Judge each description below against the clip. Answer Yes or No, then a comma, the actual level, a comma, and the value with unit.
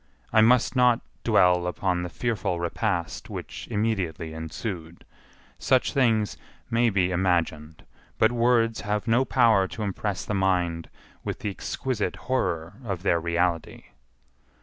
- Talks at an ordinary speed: No, slow, 130 wpm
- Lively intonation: No, average, 4.7 semitones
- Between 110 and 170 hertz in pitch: No, very low, 95 Hz